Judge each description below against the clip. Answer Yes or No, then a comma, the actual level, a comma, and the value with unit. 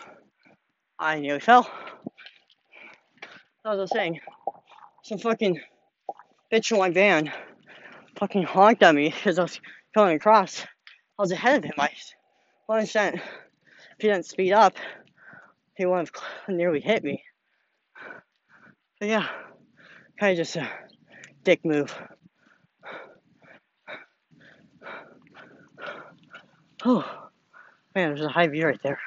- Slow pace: Yes, slow, 115 wpm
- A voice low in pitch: No, high, 200 Hz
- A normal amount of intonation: Yes, average, 4.5 semitones